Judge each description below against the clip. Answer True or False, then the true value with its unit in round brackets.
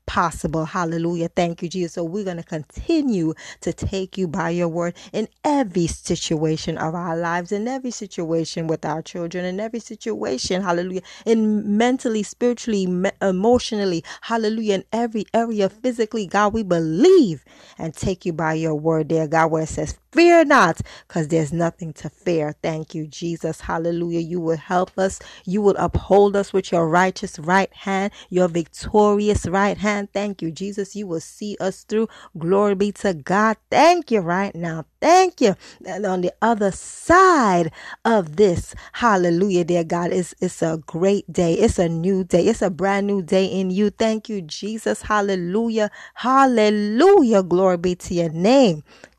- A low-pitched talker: False (190 Hz)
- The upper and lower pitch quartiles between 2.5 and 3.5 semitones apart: False (3.9 semitones)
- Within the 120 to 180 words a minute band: True (165 wpm)